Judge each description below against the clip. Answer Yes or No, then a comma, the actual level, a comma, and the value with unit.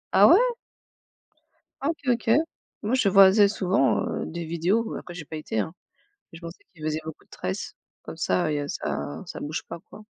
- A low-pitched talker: No, medium, 170 Hz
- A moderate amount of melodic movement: Yes, average, 4.8 semitones